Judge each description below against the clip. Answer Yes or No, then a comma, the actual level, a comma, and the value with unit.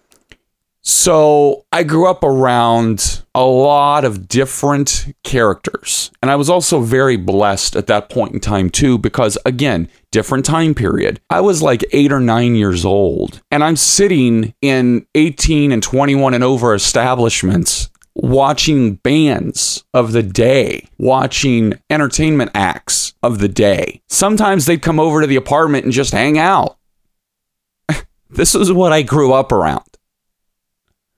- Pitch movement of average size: Yes, average, 4.3 semitones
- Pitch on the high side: No, low, 135 Hz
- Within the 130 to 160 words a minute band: Yes, average, 140 wpm